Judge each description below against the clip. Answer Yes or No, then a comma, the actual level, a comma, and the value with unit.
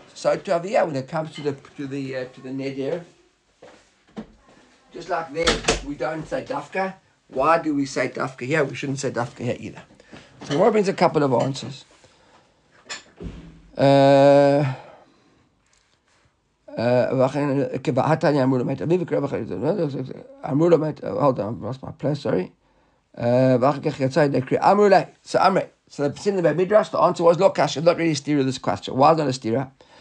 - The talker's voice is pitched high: No, medium, 140 Hz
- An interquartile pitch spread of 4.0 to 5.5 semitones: No, average, 3.5 semitones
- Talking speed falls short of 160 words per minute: Yes, average, 150 wpm